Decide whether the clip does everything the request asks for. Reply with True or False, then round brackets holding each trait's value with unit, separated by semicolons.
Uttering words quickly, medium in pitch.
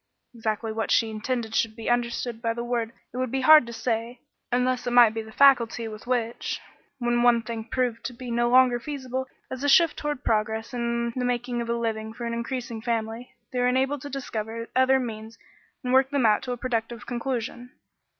False (210 wpm; 240 Hz)